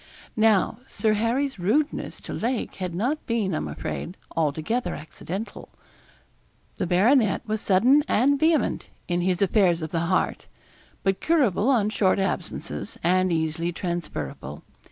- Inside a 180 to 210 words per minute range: No, slow, 135 wpm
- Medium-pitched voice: No, high, 195 Hz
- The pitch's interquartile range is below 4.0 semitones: No, average, 5.1 semitones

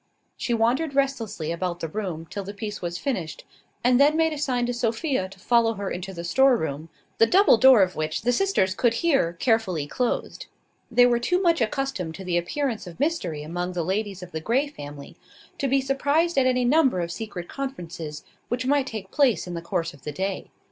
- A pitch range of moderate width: No, wide, 7.2 semitones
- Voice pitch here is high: Yes, high, 225 Hz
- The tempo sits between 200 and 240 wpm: Yes, fast, 205 wpm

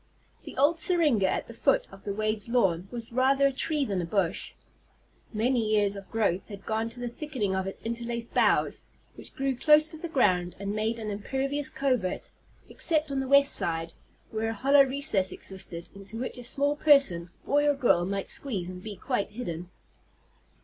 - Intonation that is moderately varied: No, wide, 5.8 semitones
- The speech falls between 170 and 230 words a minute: Yes, average, 190 wpm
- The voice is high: Yes, high, 230 Hz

